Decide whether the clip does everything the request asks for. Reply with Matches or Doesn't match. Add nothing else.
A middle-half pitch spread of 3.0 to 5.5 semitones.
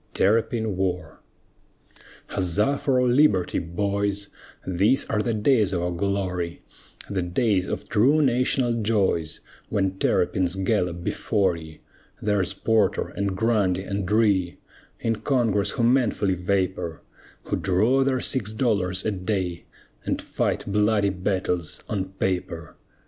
Matches